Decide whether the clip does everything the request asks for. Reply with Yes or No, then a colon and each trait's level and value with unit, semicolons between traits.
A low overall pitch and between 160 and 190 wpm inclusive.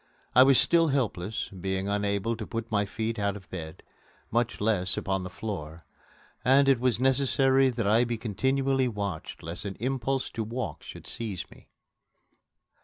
Yes: low, 110 Hz; average, 165 wpm